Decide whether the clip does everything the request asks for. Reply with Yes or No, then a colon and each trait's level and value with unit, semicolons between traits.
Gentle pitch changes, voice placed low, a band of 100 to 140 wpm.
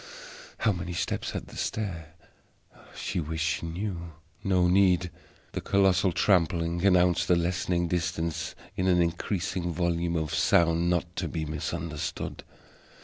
Yes: narrow, 1.5 semitones; very low, 85 Hz; slow, 135 wpm